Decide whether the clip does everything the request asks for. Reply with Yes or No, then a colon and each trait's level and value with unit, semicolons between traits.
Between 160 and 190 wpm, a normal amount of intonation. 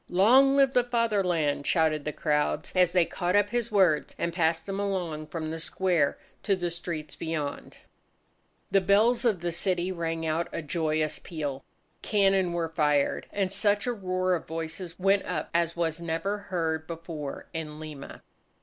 Yes: average, 165 wpm; average, 3.5 semitones